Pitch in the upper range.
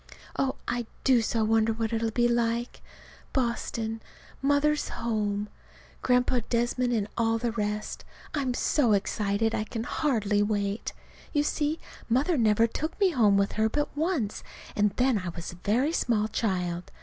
Yes: high, 230 Hz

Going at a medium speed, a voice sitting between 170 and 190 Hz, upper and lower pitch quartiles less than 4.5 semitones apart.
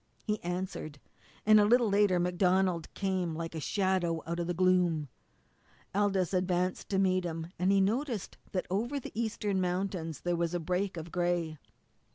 Yes: average, 170 wpm; medium, 185 Hz; narrow, 2.4 semitones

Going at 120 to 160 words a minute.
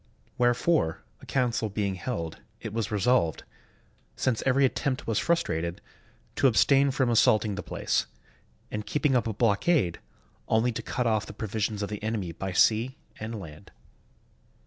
Yes: average, 150 wpm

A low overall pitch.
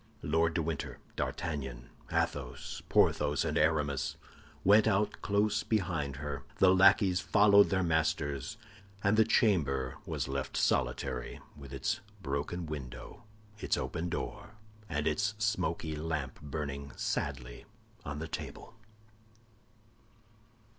Yes: very low, 80 Hz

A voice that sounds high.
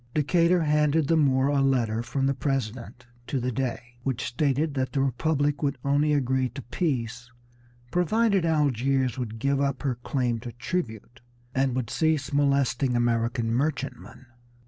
No: low, 135 Hz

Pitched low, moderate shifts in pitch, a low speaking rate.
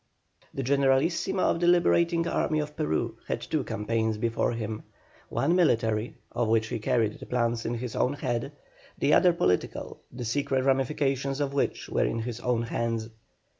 No: low, 125 Hz; average, 4.0 semitones; average, 170 wpm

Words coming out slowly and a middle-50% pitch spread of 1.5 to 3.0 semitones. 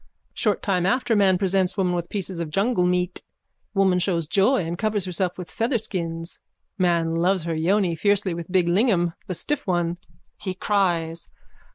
No: average, 165 wpm; narrow, 2.6 semitones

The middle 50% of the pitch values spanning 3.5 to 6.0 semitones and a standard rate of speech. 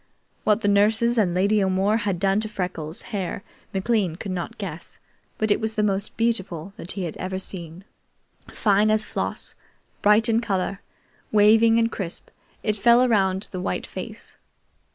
No: narrow, 2.5 semitones; average, 165 wpm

